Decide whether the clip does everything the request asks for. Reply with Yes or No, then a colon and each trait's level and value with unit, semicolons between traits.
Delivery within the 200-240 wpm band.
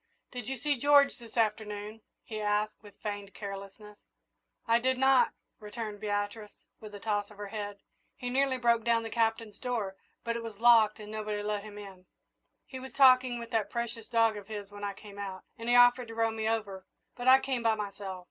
Yes: fast, 205 wpm